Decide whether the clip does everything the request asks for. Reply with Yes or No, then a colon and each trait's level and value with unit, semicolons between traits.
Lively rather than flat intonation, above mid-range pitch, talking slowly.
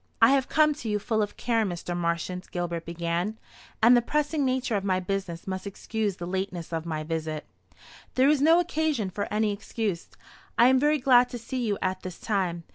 No: wide, 6.1 semitones; high, 205 Hz; average, 200 wpm